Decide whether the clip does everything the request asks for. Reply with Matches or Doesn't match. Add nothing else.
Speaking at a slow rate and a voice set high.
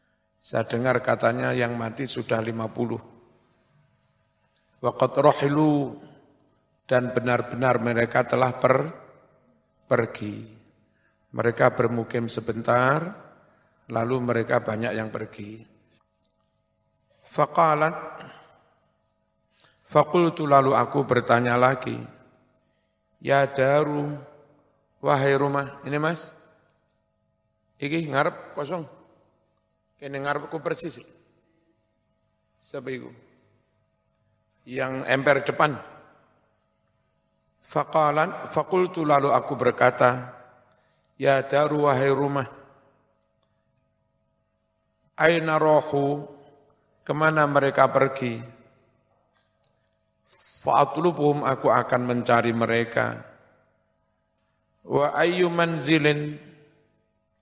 Doesn't match